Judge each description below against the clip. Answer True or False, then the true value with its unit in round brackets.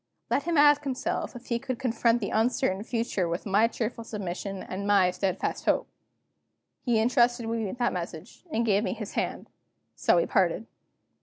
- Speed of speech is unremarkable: True (175 wpm)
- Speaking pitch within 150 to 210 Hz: False (230 Hz)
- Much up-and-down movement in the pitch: False (3.6 semitones)